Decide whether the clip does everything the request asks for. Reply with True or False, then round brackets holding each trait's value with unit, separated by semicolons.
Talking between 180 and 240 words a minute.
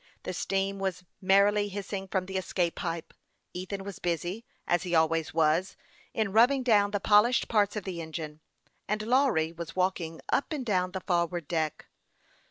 False (170 wpm)